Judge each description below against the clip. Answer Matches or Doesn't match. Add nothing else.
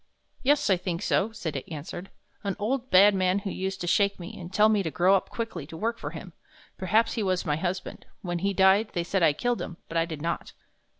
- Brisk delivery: Matches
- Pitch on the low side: Doesn't match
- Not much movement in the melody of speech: Doesn't match